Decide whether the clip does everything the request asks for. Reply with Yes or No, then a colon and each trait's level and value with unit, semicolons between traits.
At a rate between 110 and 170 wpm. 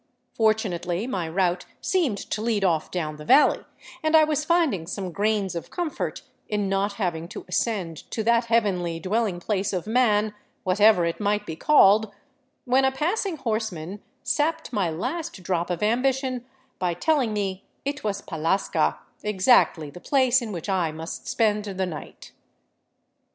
Yes: average, 160 wpm